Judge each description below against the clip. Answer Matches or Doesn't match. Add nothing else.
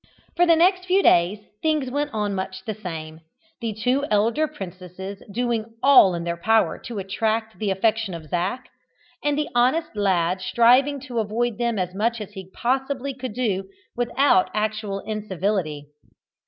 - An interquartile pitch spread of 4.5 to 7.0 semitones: Matches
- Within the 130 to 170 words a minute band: Matches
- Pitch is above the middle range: Matches